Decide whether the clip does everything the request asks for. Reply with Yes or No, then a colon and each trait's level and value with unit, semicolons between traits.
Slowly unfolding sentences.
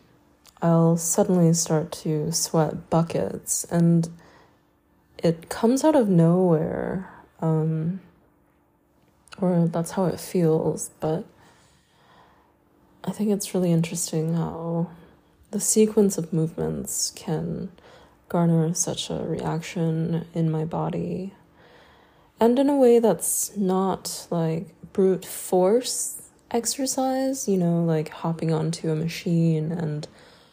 Yes: slow, 110 wpm